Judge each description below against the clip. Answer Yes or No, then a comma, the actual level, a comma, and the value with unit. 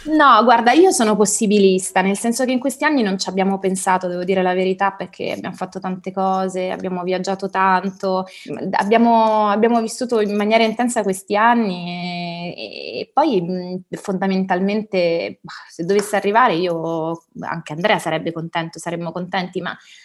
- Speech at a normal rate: Yes, average, 155 wpm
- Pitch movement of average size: Yes, average, 3.4 semitones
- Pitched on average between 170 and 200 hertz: Yes, high, 190 Hz